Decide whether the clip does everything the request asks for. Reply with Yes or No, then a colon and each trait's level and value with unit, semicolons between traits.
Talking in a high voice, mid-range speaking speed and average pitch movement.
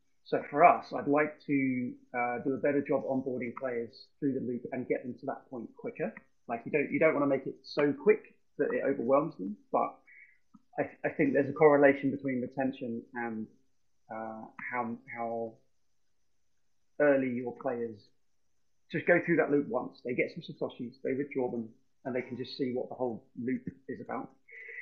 No: low, 130 Hz; average, 190 wpm; average, 3.4 semitones